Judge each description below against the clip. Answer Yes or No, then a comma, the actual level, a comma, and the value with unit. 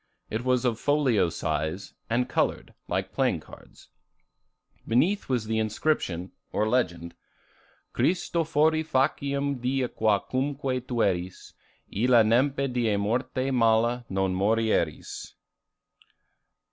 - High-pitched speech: No, low, 120 Hz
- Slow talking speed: Yes, slow, 110 wpm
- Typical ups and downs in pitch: Yes, average, 4.0 semitones